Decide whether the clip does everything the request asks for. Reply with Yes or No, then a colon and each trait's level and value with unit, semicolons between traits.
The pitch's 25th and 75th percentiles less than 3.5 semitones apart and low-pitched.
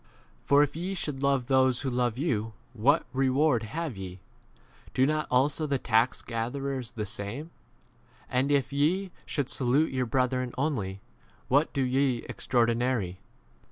Yes: average, 3.1 semitones; low, 130 Hz